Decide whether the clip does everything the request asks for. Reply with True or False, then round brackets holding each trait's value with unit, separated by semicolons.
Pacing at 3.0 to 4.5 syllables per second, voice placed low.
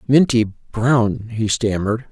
True (3.6 syllables/s; 115 Hz)